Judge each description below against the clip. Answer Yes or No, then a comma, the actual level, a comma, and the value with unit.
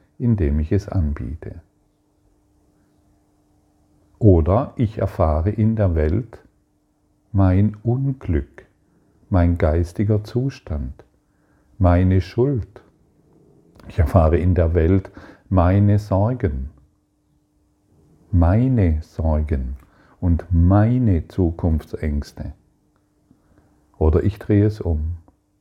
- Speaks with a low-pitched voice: Yes, very low, 95 Hz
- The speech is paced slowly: Yes, slow, 80 wpm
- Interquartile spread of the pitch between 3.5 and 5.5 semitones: Yes, average, 4.7 semitones